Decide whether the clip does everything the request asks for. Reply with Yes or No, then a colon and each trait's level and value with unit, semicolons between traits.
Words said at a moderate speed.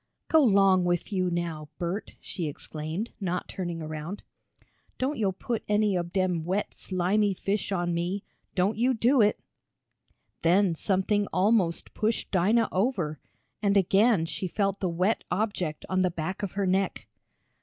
Yes: average, 155 wpm